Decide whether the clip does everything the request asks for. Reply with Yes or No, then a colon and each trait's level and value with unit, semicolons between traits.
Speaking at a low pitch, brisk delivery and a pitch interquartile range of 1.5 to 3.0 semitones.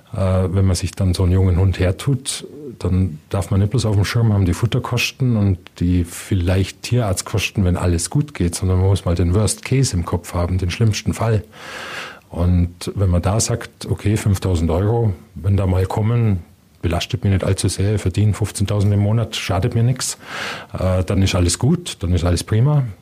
No: low, 100 Hz; fast, 195 wpm; average, 3.6 semitones